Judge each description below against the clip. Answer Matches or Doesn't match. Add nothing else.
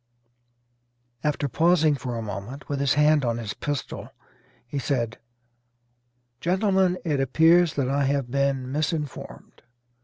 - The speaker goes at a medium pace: Doesn't match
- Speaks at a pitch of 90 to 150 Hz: Matches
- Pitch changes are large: Doesn't match